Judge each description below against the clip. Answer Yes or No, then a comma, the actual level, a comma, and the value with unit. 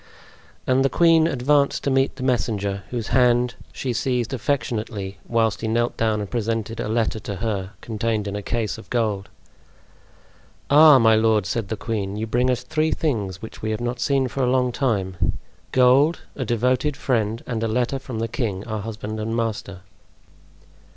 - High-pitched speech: No, low, 115 Hz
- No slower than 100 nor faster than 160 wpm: No, average, 180 wpm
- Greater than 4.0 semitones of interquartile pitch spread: No, average, 3.0 semitones